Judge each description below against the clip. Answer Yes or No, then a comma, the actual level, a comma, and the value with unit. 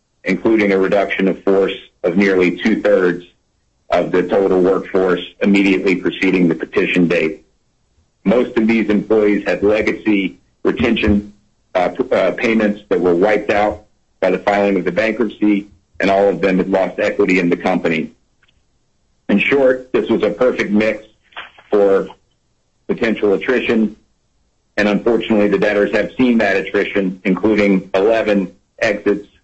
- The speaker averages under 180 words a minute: Yes, average, 145 wpm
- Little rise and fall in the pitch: Yes, narrow, 1.8 semitones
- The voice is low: Yes, low, 100 Hz